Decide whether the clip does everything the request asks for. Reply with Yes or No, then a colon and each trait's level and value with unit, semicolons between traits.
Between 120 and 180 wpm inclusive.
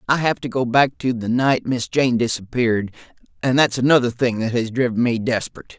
No: average, 195 wpm